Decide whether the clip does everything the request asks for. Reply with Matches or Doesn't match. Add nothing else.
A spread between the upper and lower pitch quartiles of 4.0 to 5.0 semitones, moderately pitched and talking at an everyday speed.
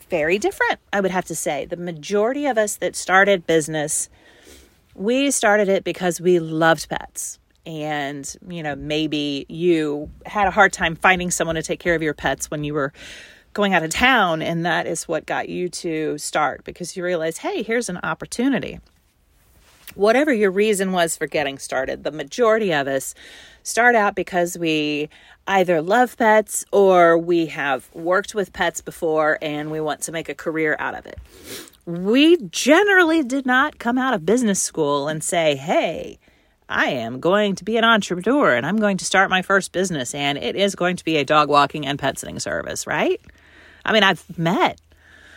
Matches